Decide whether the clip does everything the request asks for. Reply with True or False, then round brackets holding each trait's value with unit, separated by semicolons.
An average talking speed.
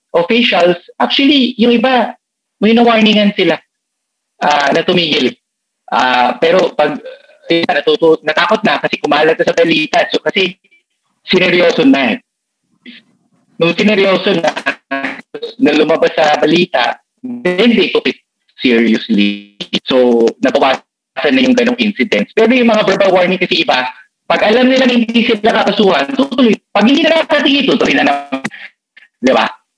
True (135 wpm)